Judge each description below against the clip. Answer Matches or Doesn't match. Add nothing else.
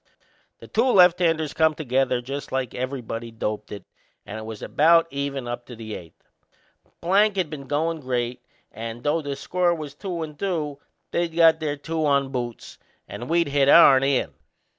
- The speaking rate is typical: Matches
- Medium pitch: Matches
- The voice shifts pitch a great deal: Doesn't match